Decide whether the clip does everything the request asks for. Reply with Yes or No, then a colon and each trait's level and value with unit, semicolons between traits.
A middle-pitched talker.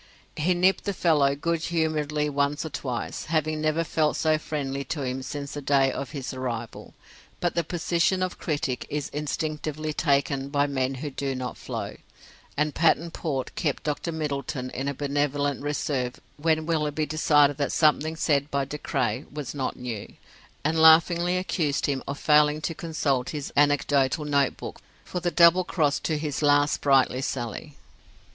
Yes: medium, 145 Hz